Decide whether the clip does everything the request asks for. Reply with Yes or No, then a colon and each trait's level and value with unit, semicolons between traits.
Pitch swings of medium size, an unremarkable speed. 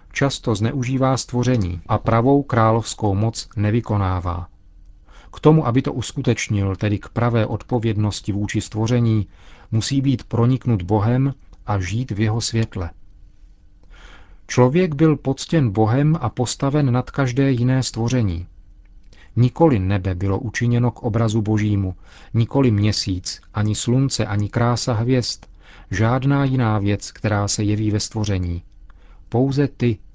Yes: average, 4.0 semitones; average, 125 wpm